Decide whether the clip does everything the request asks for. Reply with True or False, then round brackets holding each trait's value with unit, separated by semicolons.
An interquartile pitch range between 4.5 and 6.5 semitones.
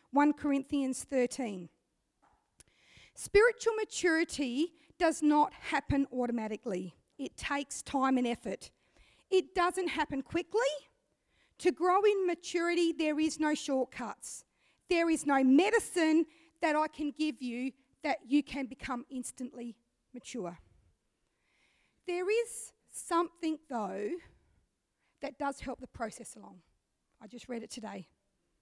True (5.0 semitones)